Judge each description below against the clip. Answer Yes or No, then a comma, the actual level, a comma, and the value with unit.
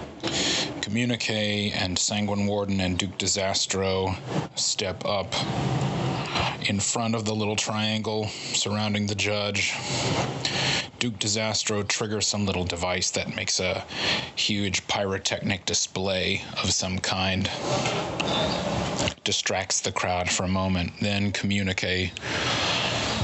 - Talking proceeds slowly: Yes, slow, 105 wpm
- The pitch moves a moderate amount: No, narrow, 2.2 semitones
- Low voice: Yes, low, 100 Hz